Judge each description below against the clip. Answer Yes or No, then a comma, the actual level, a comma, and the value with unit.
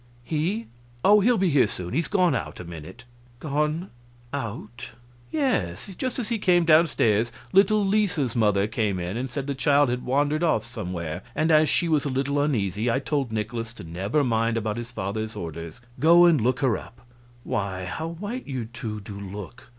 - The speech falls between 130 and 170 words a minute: No, average, 190 wpm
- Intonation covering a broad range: Yes, wide, 7.0 semitones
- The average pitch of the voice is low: Yes, low, 125 Hz